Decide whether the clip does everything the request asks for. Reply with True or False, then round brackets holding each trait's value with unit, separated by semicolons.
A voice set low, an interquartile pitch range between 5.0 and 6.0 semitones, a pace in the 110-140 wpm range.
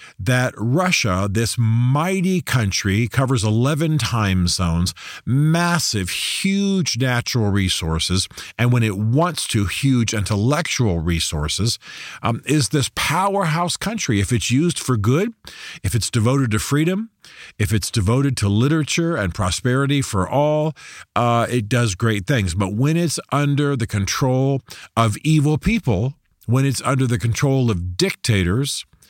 True (120 Hz; 5.5 semitones; 135 wpm)